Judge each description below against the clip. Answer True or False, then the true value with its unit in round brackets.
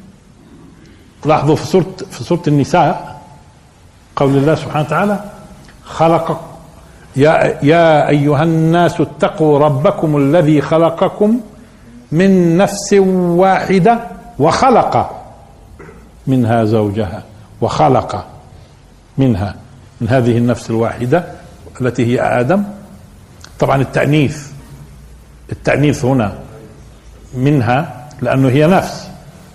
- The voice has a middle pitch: True (150 Hz)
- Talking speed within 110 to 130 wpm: False (85 wpm)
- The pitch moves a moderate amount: False (6.0 semitones)